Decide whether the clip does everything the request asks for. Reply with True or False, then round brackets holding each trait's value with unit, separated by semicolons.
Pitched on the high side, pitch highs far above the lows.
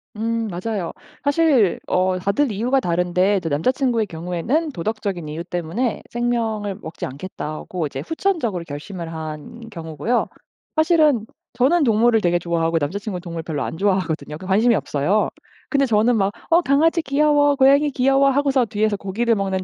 True (210 Hz; 6.8 semitones)